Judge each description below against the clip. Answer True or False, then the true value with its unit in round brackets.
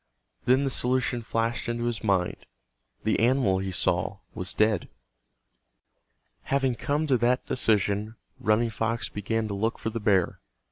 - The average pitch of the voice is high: False (110 Hz)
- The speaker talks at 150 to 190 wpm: False (140 wpm)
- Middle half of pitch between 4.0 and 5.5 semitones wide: False (3.4 semitones)